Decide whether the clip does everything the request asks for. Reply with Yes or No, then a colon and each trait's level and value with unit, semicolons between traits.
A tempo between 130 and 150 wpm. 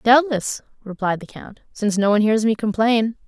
No: average, 185 wpm